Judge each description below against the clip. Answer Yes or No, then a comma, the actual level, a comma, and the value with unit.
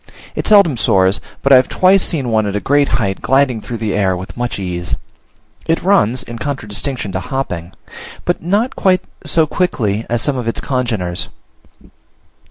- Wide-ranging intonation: Yes, wide, 6.0 semitones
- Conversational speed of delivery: Yes, average, 175 wpm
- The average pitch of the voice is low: Yes, low, 120 Hz